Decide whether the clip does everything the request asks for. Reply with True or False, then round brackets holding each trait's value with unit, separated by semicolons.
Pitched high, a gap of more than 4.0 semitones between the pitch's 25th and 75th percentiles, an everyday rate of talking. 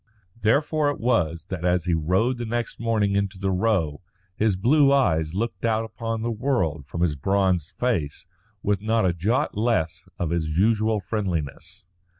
False (100 Hz; 5.1 semitones; 165 wpm)